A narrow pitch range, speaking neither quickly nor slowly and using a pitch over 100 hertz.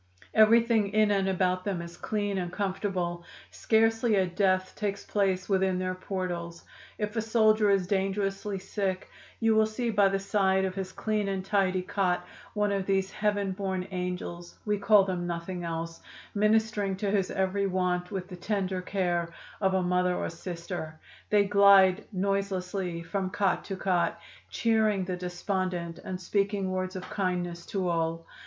Yes: narrow, 1.9 semitones; average, 160 wpm; high, 190 Hz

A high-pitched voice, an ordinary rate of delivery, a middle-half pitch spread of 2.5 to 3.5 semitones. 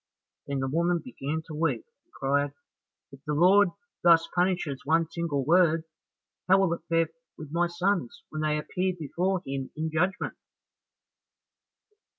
No: medium, 165 Hz; average, 150 wpm; average, 3.0 semitones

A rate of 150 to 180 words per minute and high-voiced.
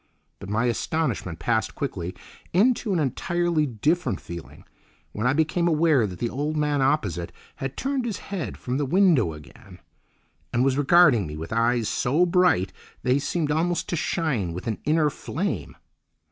No: average, 160 wpm; medium, 140 Hz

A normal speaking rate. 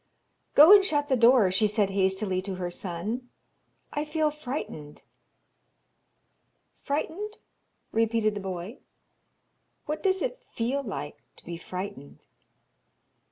No: slow, 115 wpm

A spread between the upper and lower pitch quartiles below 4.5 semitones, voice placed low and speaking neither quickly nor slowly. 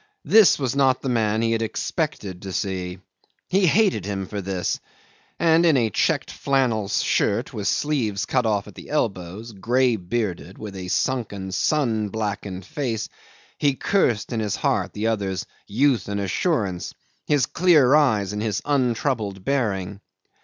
No: average, 5.2 semitones; low, 110 Hz; average, 155 wpm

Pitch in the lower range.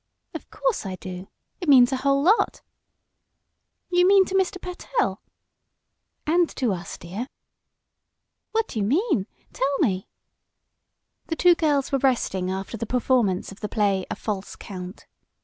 No: very high, 255 Hz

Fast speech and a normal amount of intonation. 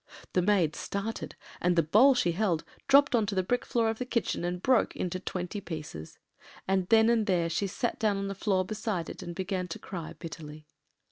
Yes: fast, 210 wpm; average, 4.2 semitones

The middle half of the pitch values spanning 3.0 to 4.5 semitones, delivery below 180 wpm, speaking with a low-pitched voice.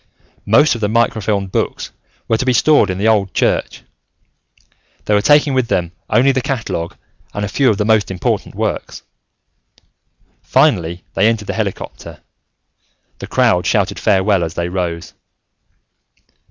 Yes: average, 3.8 semitones; average, 150 wpm; low, 105 Hz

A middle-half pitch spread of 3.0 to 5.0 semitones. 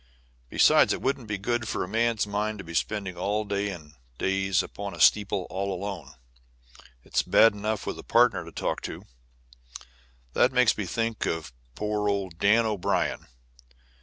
No: narrow, 2.4 semitones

